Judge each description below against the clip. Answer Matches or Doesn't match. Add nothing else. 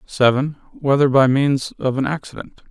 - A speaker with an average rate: Matches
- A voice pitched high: Doesn't match